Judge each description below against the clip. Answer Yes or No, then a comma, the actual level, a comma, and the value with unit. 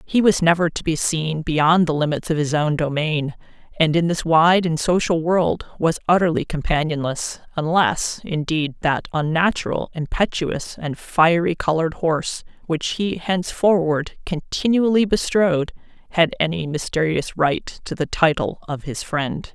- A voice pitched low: No, medium, 165 Hz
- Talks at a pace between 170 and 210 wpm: No, average, 140 wpm